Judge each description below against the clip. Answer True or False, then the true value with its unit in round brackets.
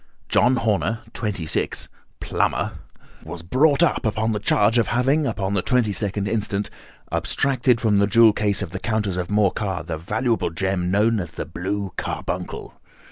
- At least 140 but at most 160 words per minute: True (155 wpm)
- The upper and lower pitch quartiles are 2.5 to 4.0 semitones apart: True (3.3 semitones)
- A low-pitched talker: True (105 Hz)